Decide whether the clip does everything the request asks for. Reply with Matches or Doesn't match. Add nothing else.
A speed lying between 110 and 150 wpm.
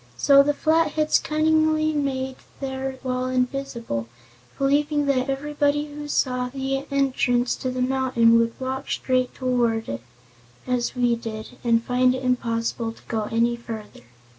Matches